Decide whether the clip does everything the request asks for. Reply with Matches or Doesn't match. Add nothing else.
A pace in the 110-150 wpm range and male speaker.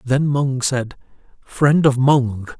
Matches